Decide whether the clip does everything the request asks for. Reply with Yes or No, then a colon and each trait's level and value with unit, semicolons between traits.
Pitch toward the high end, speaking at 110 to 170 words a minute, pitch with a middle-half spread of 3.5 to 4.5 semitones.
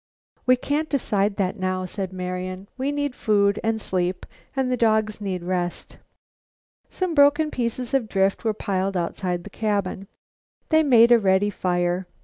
No: high, 205 Hz; average, 155 wpm; average, 4.9 semitones